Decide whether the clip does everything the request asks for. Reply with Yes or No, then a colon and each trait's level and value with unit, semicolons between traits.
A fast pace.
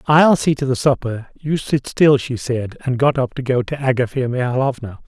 Yes: fast, 215 wpm